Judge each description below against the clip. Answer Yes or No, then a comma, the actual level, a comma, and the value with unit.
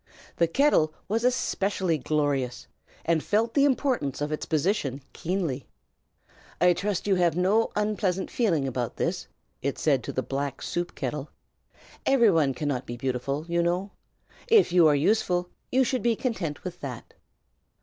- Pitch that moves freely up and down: Yes, wide, 6.4 semitones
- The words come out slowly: No, average, 155 wpm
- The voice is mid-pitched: Yes, medium, 170 Hz